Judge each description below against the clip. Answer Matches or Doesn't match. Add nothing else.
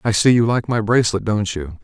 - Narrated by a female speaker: Doesn't match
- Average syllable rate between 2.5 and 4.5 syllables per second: Doesn't match